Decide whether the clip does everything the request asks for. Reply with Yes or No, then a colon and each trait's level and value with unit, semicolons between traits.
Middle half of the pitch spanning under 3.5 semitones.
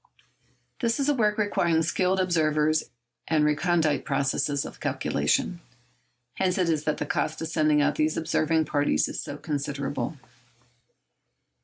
Yes: average, 2.8 semitones